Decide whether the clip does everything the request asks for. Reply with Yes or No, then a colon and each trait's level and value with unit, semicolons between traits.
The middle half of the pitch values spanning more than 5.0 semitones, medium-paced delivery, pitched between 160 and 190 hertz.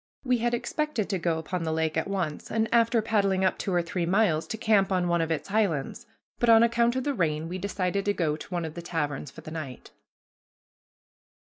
No: wide, 5.4 semitones; fast, 225 wpm; medium, 185 Hz